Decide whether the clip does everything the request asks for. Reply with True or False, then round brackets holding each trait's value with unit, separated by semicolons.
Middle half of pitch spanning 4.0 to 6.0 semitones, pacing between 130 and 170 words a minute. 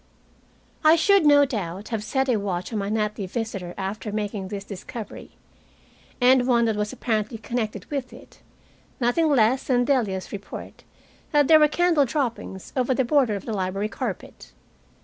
True (4.5 semitones; 165 wpm)